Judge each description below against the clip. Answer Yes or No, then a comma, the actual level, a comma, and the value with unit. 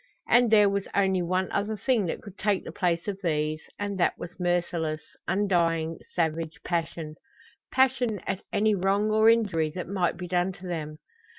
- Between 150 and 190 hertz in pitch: Yes, medium, 185 Hz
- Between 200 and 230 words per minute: No, average, 175 wpm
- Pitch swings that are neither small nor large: Yes, average, 3.5 semitones